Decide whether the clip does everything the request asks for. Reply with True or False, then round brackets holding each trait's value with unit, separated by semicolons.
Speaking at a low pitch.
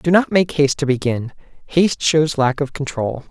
False (145 Hz)